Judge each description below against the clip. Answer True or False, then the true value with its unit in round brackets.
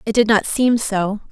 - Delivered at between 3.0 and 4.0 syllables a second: False (4.5 syllables/s)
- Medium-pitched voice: False (215 Hz)